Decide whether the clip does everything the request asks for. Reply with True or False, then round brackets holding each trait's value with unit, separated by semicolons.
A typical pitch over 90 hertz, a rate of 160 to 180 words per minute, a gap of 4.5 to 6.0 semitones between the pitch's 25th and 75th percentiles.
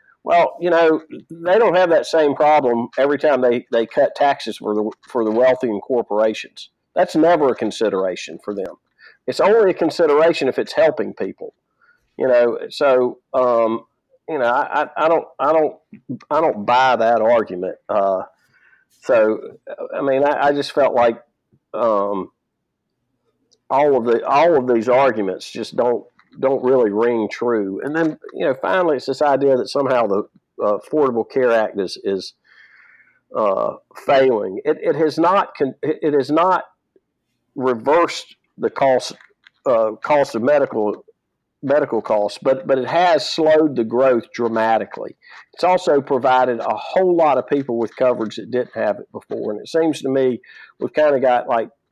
True (130 Hz; 165 wpm; 5.1 semitones)